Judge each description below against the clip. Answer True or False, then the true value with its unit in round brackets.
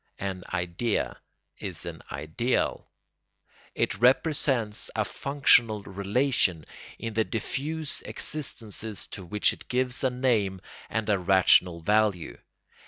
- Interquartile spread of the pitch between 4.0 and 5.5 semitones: True (4.8 semitones)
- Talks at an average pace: False (110 wpm)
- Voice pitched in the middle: False (110 Hz)